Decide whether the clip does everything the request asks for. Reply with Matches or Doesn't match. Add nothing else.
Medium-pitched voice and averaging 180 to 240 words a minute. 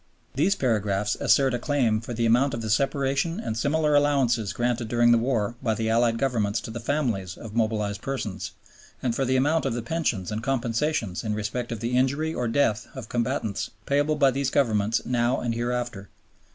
Doesn't match